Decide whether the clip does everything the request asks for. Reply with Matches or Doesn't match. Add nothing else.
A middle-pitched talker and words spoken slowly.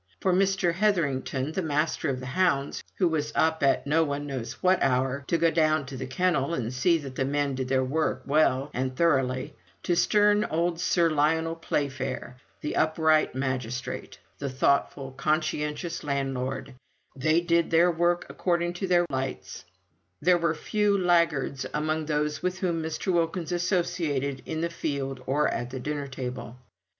Doesn't match